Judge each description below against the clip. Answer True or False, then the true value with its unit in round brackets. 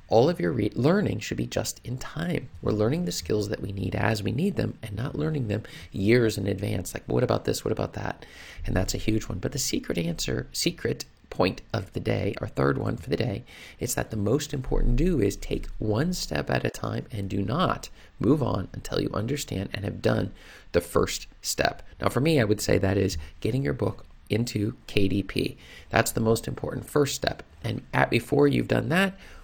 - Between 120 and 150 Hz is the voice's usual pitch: False (105 Hz)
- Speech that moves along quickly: True (220 wpm)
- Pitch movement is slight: False (5.1 semitones)